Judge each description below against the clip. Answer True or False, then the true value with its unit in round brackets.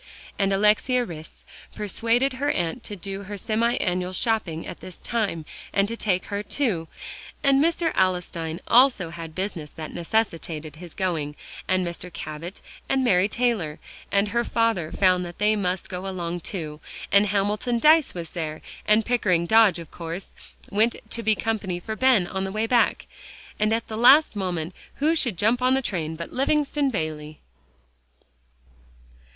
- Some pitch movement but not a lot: True (5.0 semitones)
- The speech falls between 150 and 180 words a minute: True (160 wpm)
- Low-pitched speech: False (195 Hz)